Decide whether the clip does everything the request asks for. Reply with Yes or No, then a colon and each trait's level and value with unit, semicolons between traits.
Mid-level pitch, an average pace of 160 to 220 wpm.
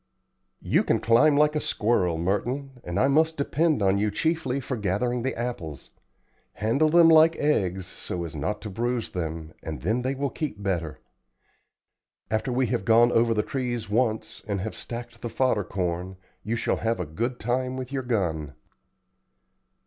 No: low, 115 Hz; average, 170 wpm